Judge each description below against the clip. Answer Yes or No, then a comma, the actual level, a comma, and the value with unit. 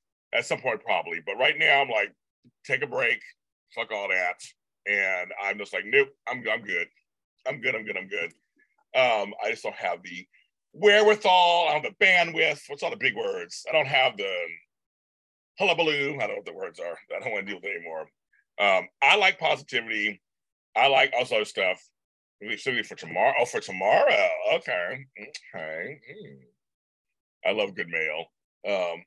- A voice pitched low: No, very high, 330 Hz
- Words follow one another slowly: No, average, 190 wpm